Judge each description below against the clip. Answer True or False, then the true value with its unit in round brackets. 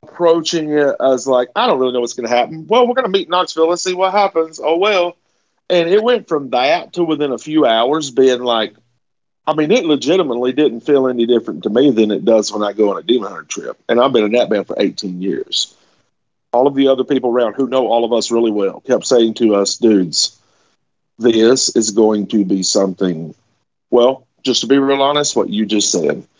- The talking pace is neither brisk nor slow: False (225 wpm)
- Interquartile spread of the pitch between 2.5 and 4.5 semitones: False (5.6 semitones)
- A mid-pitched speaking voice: False (130 Hz)